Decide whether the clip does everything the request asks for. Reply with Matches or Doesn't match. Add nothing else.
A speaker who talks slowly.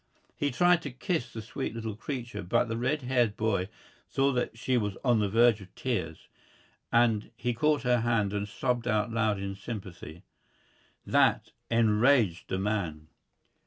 Doesn't match